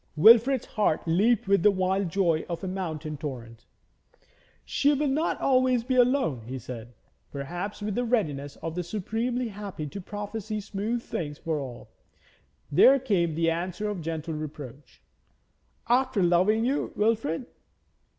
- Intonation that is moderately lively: No, wide, 6.3 semitones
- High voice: Yes, high, 195 Hz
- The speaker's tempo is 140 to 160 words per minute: Yes, average, 145 wpm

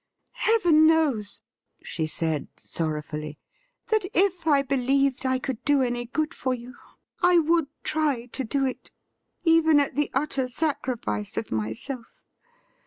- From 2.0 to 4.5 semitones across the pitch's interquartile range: No, average, 5.1 semitones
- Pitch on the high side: Yes, very high, 270 Hz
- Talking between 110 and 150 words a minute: Yes, average, 145 wpm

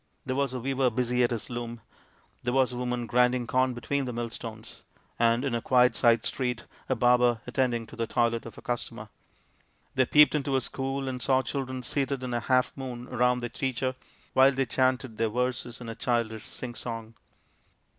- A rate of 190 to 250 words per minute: Yes, average, 195 wpm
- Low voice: Yes, low, 125 Hz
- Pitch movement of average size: No, narrow, 1.7 semitones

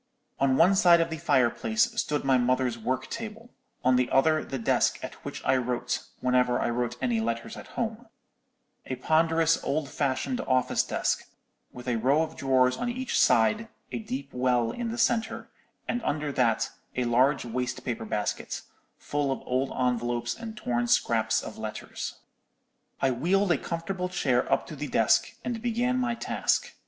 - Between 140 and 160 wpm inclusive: No, average, 170 wpm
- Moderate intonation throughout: No, wide, 7.9 semitones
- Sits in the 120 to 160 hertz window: Yes, low, 135 Hz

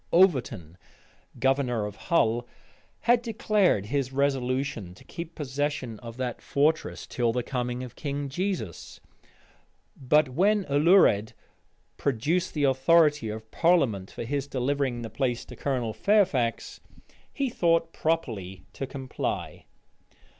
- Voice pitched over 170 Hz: No, low, 135 Hz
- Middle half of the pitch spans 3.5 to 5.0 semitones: No, wide, 5.4 semitones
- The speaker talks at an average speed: No, slow, 120 wpm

